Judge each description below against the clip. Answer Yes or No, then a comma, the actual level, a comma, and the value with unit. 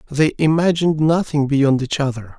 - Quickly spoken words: No, average, 150 wpm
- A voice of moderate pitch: Yes, medium, 145 Hz